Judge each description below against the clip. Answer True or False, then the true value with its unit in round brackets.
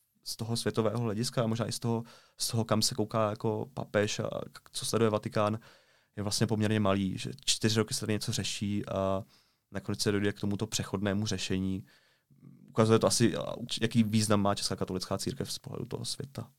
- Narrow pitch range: True (1.9 semitones)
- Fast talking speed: True (190 wpm)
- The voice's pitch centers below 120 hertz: True (110 Hz)